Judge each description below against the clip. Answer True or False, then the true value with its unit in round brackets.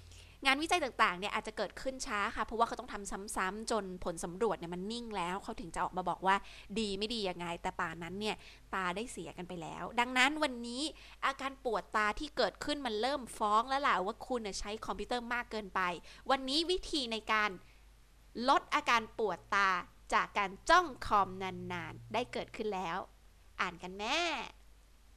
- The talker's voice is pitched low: False (215 Hz)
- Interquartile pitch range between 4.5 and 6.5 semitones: True (5.0 semitones)